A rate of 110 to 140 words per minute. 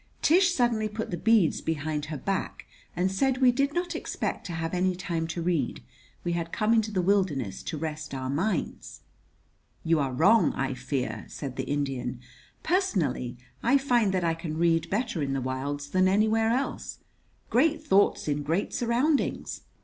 No: average, 170 wpm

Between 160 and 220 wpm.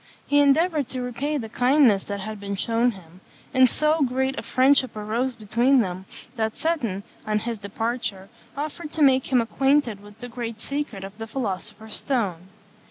Yes: average, 170 wpm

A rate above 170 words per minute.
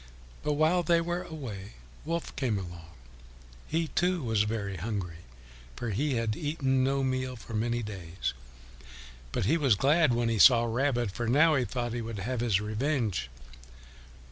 No: average, 165 wpm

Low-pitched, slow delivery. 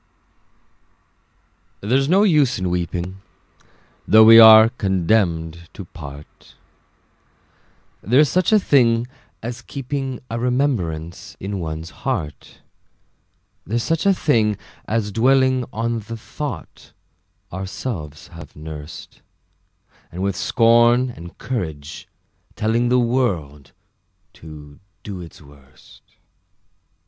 Yes: low, 110 Hz; slow, 100 wpm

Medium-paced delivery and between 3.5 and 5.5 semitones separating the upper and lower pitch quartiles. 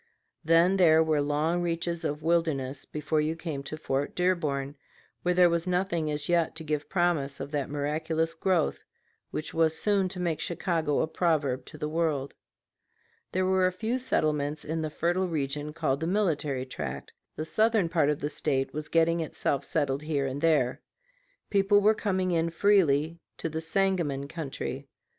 No: average, 170 wpm; average, 3.1 semitones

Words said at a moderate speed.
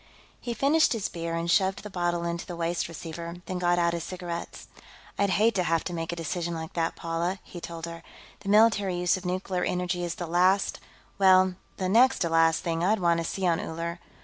No: fast, 220 wpm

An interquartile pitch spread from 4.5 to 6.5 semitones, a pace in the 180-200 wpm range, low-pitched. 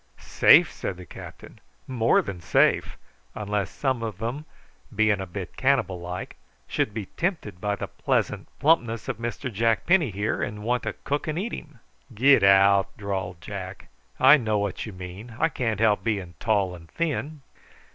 No: average, 4.9 semitones; average, 170 wpm; low, 110 Hz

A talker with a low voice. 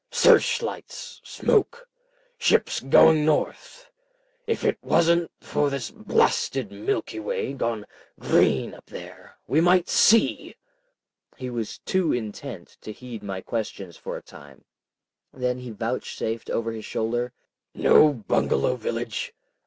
Yes: low, 125 Hz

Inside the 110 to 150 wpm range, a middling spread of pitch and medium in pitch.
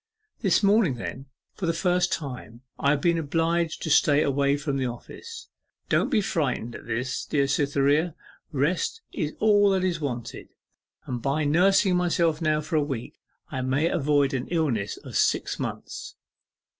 No: average, 165 wpm; average, 4.1 semitones; medium, 150 Hz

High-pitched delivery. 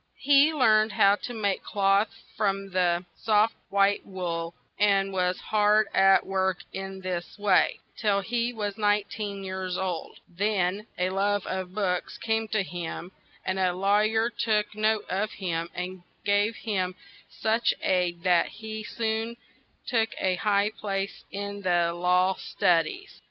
Yes: high, 200 Hz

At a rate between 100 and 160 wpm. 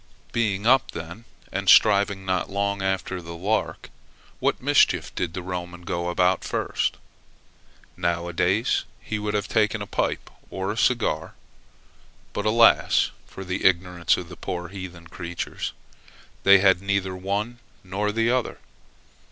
Yes: average, 145 wpm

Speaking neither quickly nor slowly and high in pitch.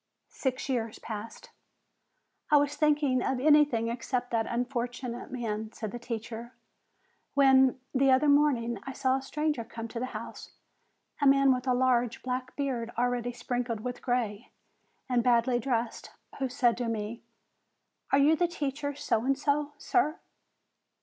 Yes: average, 150 wpm; very high, 250 Hz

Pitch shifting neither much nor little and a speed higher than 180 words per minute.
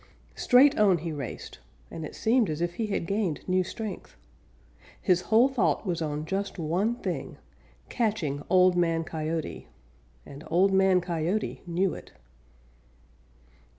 No: average, 4.1 semitones; average, 140 wpm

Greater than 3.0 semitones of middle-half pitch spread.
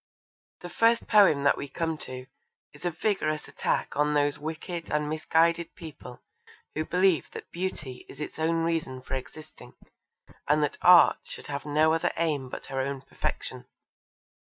No: narrow, 2.6 semitones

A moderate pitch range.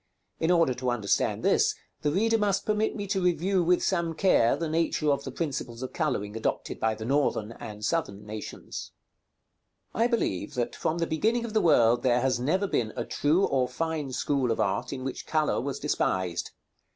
No: wide, 6.9 semitones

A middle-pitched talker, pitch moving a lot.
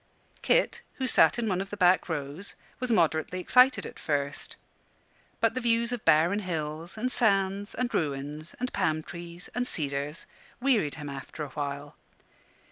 Yes: medium, 175 Hz; wide, 7.1 semitones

